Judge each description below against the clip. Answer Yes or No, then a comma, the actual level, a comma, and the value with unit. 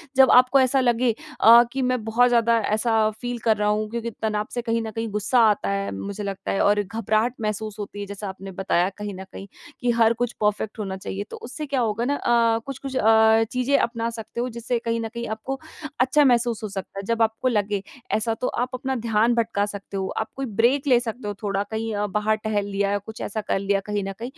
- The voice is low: No, high, 220 Hz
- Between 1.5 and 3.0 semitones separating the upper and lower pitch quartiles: Yes, average, 2.7 semitones